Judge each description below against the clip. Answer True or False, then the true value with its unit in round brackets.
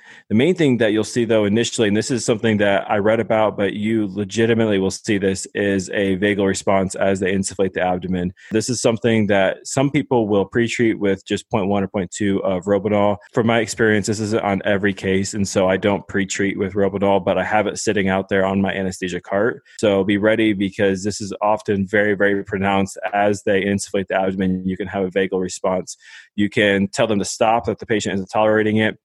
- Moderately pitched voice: False (100 Hz)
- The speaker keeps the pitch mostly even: True (1.9 semitones)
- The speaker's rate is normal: False (220 wpm)